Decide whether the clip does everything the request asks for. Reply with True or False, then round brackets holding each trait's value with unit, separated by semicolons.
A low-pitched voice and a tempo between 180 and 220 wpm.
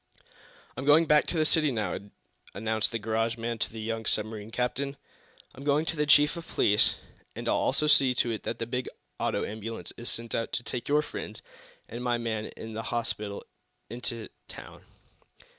True (115 Hz; 190 wpm)